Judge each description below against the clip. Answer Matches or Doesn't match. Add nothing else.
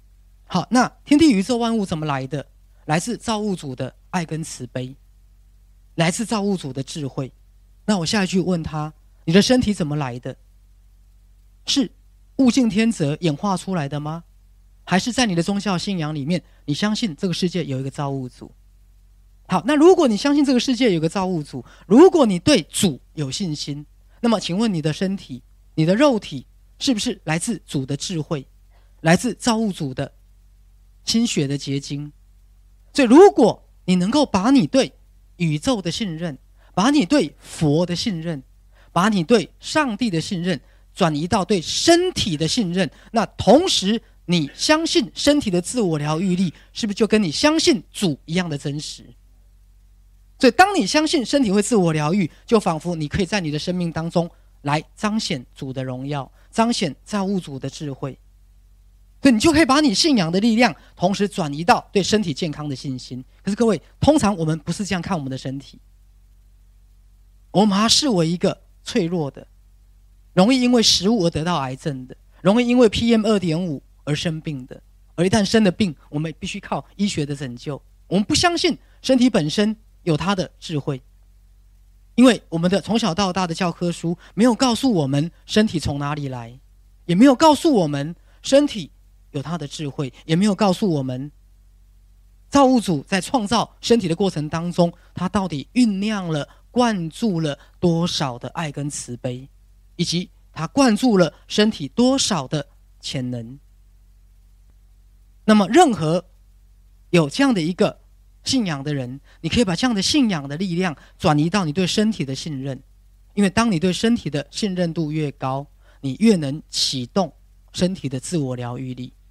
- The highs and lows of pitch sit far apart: Matches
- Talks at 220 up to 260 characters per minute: Matches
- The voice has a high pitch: Doesn't match